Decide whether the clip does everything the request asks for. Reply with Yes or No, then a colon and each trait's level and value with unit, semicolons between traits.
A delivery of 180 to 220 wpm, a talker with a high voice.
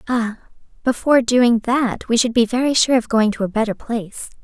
Yes: fast, 205 wpm; high, 235 Hz